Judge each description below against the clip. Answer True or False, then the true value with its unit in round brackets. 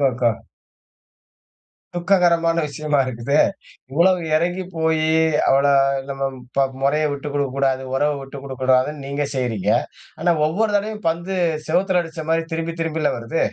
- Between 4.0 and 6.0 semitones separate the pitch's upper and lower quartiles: False (3.6 semitones)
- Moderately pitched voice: True (155 Hz)